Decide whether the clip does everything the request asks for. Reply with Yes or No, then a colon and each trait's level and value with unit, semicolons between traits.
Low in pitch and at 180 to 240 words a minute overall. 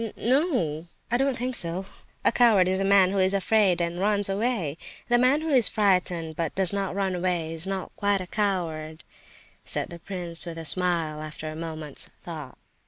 No: medium, 185 Hz; average, 190 wpm